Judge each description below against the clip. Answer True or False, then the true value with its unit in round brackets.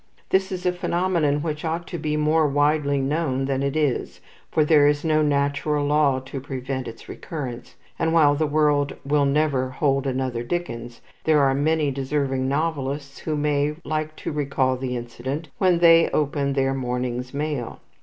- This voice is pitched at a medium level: True (145 Hz)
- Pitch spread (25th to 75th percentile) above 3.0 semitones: False (2.5 semitones)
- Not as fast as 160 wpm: False (170 wpm)